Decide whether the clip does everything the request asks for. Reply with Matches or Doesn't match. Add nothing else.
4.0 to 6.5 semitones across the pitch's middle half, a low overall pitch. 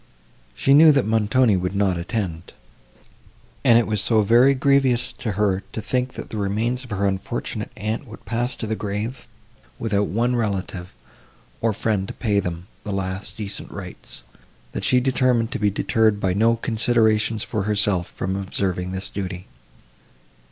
Doesn't match